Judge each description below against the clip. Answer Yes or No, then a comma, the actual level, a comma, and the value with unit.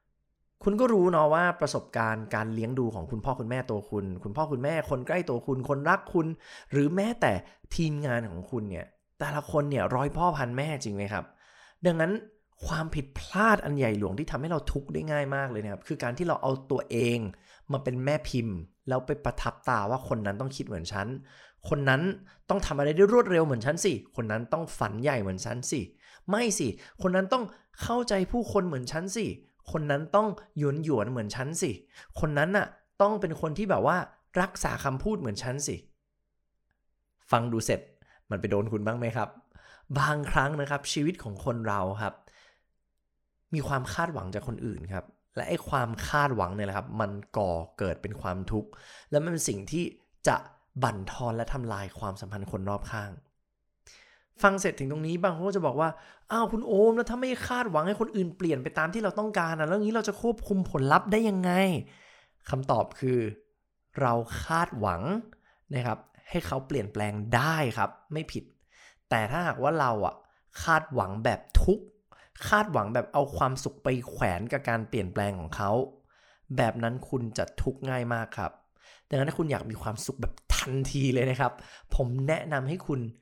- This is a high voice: No, low, 135 Hz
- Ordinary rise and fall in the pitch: No, wide, 6.8 semitones